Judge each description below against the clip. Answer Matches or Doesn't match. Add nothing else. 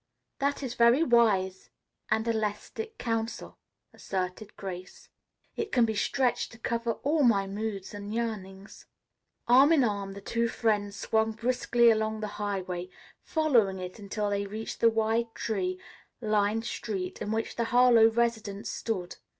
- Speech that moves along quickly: Doesn't match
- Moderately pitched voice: Doesn't match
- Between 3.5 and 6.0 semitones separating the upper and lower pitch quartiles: Doesn't match